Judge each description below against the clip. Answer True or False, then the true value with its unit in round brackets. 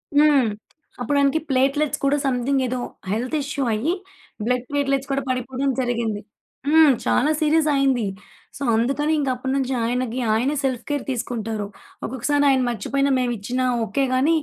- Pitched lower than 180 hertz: False (265 Hz)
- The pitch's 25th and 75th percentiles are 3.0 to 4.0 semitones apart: False (2.5 semitones)